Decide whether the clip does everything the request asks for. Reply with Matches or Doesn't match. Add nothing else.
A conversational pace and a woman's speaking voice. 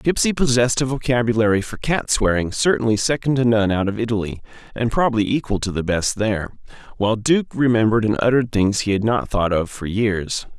Doesn't match